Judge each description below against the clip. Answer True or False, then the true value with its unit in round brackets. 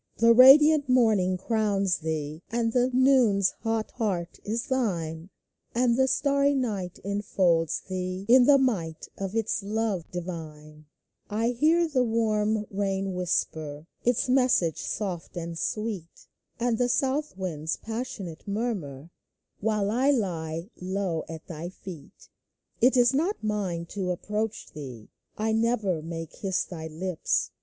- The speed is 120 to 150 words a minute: True (135 wpm)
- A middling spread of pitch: False (5.7 semitones)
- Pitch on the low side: False (200 Hz)